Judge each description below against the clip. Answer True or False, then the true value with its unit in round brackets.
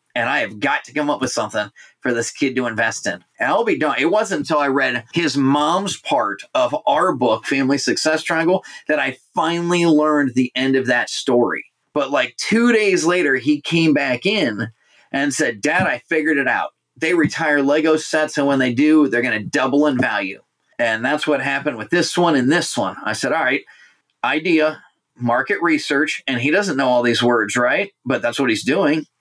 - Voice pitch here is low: False (145 Hz)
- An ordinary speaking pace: False (210 wpm)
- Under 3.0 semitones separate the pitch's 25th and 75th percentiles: False (3.6 semitones)